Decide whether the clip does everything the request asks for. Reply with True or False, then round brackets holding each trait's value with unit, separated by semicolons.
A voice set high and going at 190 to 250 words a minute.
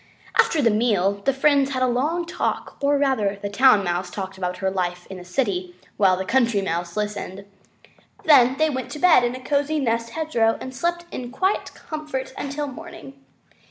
True (245 Hz; 200 wpm)